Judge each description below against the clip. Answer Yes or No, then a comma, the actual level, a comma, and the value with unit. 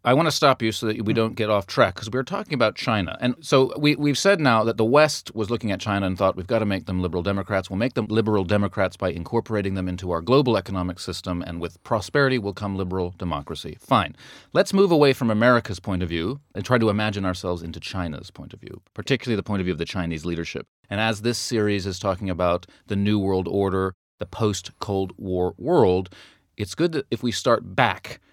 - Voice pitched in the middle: No, low, 105 Hz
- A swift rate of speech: Yes, fast, 235 wpm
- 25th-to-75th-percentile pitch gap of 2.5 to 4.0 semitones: No, average, 4.5 semitones